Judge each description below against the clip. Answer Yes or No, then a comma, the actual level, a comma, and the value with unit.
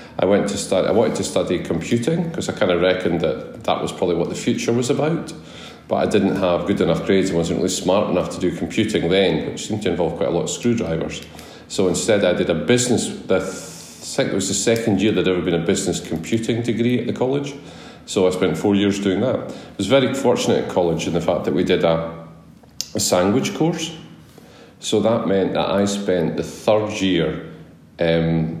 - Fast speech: Yes, fast, 220 wpm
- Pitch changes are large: Yes, wide, 5.9 semitones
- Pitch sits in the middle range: No, low, 100 Hz